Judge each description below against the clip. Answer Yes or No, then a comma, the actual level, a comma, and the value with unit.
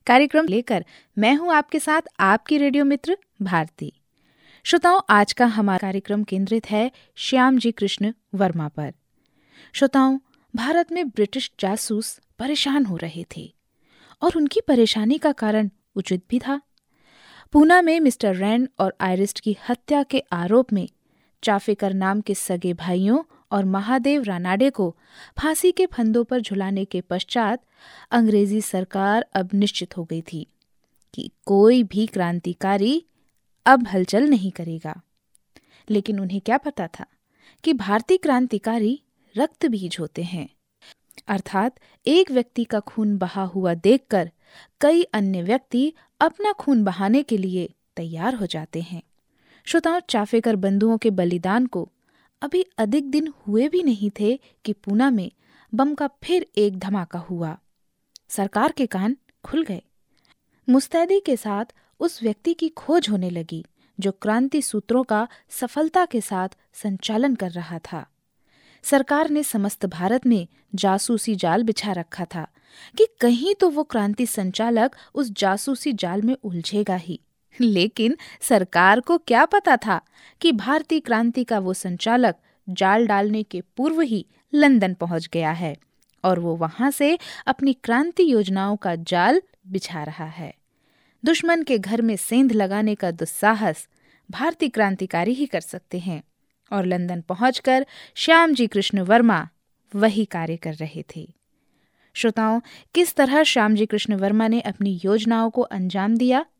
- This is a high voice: Yes, high, 220 Hz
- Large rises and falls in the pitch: Yes, wide, 5.8 semitones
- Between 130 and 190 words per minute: Yes, average, 140 wpm